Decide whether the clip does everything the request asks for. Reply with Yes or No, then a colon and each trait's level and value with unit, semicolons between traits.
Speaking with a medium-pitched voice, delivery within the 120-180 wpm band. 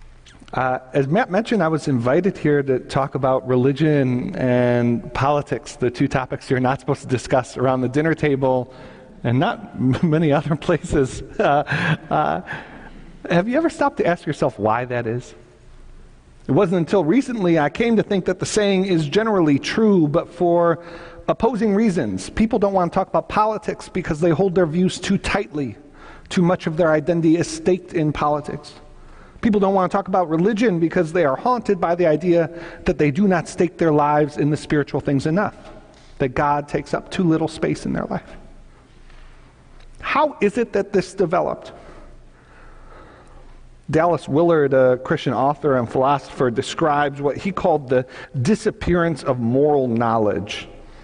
Yes: medium, 160 Hz; average, 165 wpm